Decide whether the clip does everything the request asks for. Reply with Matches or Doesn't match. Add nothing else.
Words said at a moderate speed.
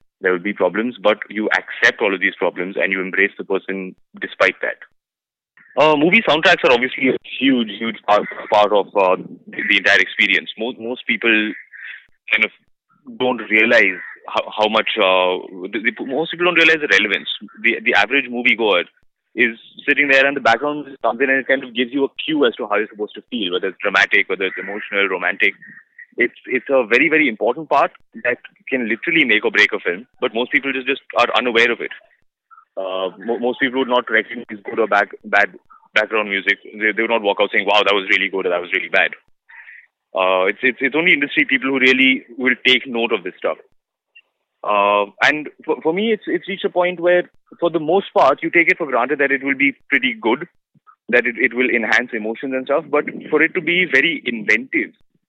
Doesn't match